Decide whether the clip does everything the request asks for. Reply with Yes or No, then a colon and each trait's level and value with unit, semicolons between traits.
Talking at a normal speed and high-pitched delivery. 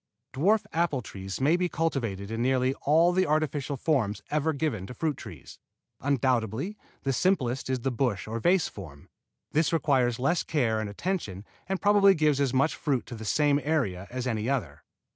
No: average, 180 wpm; low, 135 Hz